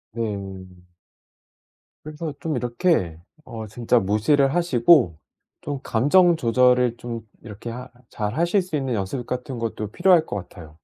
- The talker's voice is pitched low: Yes, low, 120 Hz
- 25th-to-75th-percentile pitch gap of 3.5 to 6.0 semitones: Yes, wide, 5.7 semitones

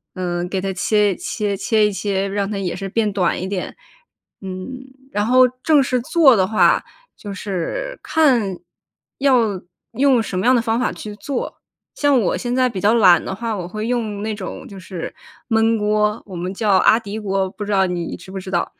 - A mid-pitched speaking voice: No, high, 210 Hz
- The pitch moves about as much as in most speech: Yes, average, 3.5 semitones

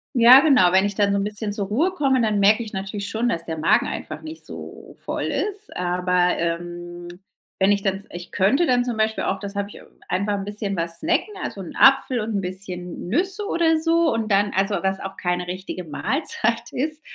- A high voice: Yes, high, 205 Hz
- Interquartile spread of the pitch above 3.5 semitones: Yes, average, 5.1 semitones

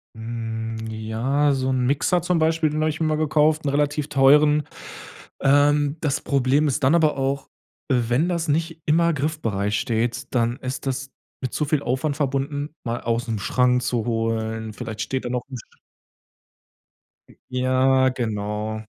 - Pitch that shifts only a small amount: No, average, 4.0 semitones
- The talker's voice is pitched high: No, low, 135 Hz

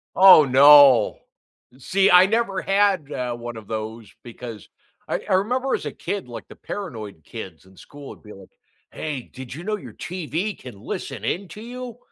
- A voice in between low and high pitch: Yes, medium, 145 Hz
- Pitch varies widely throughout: Yes, wide, 8.9 semitones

